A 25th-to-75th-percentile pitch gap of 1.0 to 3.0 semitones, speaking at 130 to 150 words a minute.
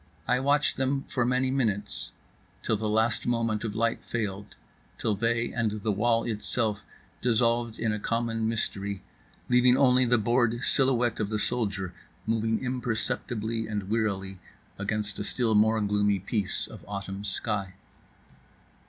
Yes: narrow, 2.6 semitones; average, 145 wpm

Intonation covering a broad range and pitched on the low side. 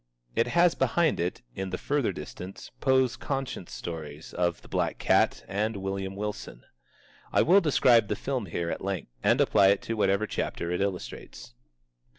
Yes: wide, 6.1 semitones; low, 100 Hz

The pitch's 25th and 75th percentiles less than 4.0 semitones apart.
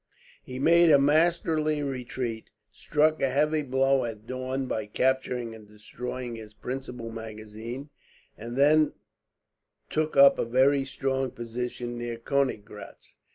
Yes: average, 3.3 semitones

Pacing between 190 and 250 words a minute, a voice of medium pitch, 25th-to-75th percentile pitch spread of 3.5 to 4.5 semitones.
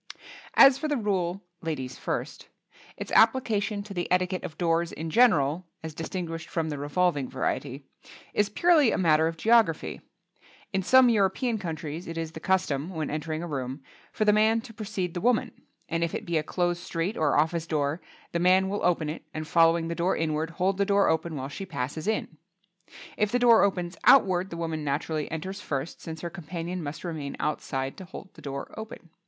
Yes: average, 195 wpm; medium, 170 Hz; average, 4.0 semitones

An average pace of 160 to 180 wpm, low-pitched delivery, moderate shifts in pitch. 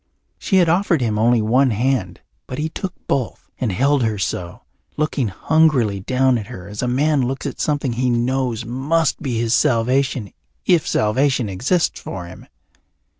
Yes: average, 170 wpm; low, 125 Hz; average, 4.3 semitones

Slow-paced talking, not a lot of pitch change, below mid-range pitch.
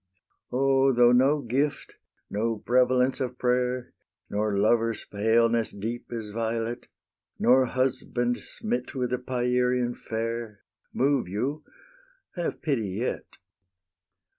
Yes: slow, 110 wpm; narrow, 2.1 semitones; low, 120 Hz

